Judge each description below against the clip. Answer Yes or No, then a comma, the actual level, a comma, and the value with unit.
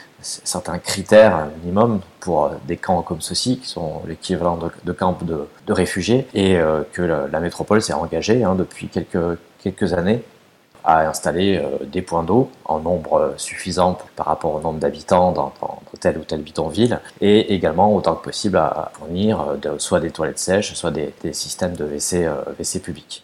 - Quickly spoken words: No, average, 170 wpm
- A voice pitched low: Yes, very low, 90 Hz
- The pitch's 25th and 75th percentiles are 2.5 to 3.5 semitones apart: Yes, average, 2.9 semitones